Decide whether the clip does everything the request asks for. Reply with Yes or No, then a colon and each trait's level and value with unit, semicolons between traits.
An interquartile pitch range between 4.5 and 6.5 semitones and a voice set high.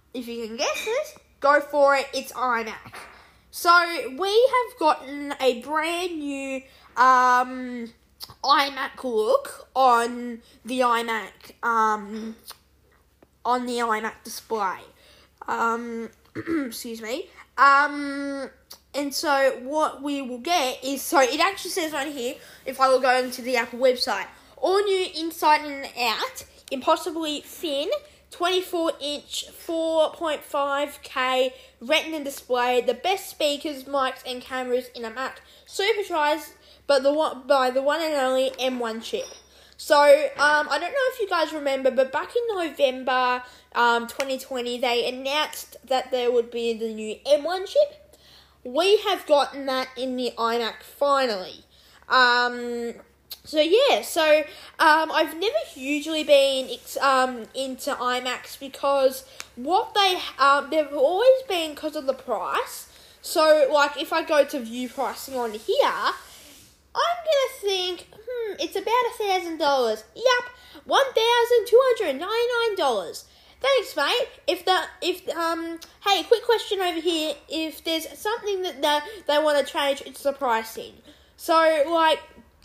Yes: average, 5.1 semitones; very high, 285 Hz